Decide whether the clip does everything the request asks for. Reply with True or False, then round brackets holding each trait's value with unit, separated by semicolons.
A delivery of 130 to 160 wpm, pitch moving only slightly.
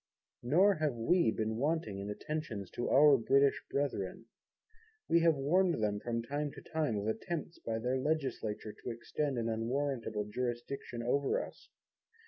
False (150 wpm; 5.0 semitones)